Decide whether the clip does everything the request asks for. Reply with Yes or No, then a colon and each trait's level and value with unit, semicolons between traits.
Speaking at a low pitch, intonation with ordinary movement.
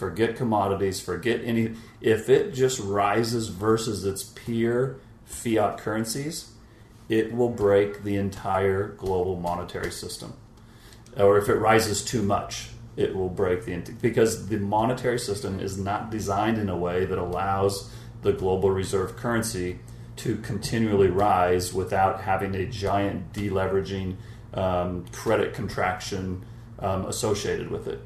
Yes: low, 105 Hz; average, 3.0 semitones